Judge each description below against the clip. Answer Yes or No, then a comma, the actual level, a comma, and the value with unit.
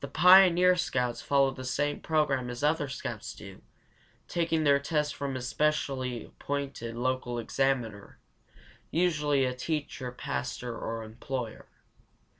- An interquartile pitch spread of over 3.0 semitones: Yes, average, 3.5 semitones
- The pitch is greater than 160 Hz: No, low, 135 Hz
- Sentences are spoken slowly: Yes, slow, 120 wpm